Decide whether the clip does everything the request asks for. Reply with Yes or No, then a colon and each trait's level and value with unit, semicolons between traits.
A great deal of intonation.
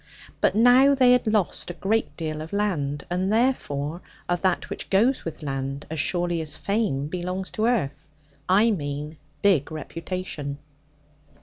Yes: wide, 5.8 semitones